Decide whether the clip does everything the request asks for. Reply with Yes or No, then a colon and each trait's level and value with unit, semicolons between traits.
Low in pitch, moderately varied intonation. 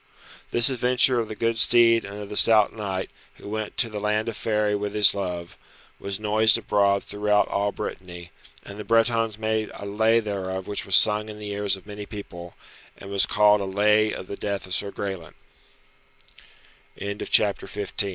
No: low, 105 Hz; narrow, 1.5 semitones